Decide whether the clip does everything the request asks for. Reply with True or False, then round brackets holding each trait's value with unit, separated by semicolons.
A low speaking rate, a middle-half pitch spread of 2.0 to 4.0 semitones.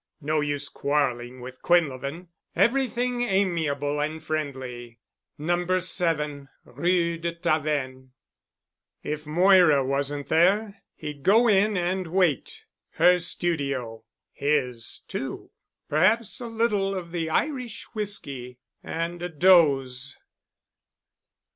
False (105 wpm; 4.7 semitones)